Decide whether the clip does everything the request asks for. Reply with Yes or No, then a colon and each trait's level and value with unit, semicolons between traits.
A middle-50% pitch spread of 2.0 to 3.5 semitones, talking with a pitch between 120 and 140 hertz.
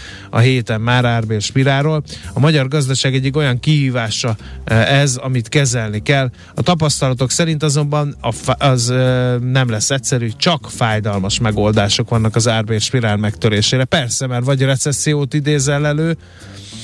No: average, 4.2 semitones; low, 125 Hz